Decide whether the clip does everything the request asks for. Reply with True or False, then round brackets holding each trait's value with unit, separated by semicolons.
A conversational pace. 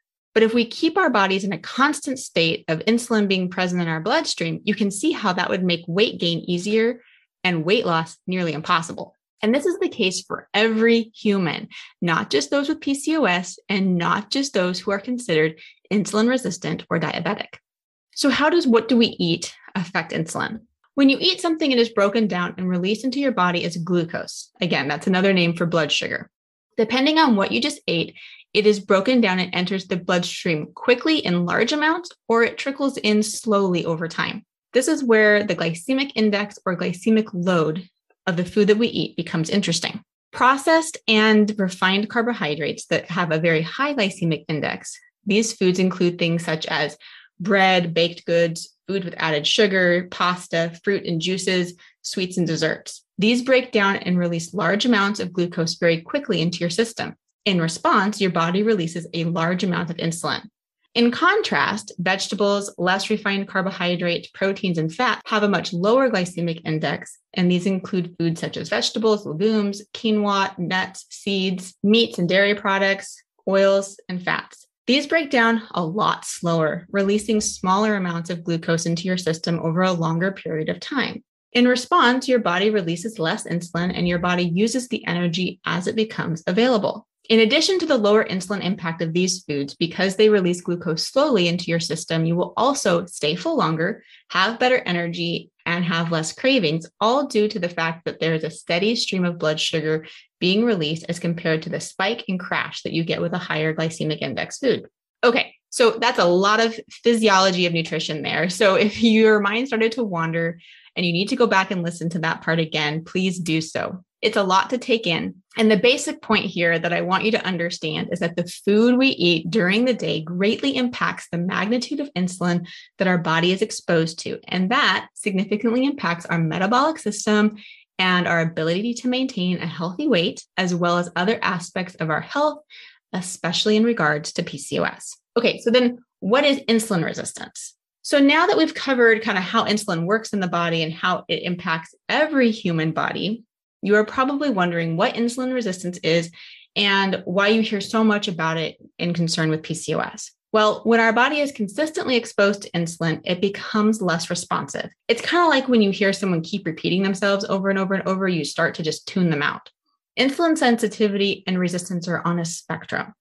True (185 wpm)